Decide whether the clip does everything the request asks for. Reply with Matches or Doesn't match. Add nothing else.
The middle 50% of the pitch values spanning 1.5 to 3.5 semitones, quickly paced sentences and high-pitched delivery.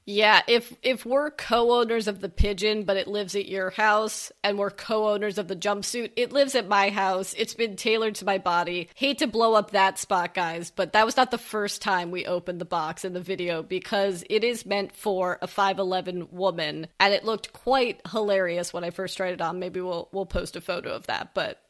Matches